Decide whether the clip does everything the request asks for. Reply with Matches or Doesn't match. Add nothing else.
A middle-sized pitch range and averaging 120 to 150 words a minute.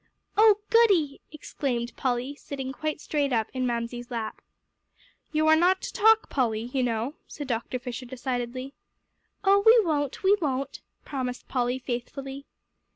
Matches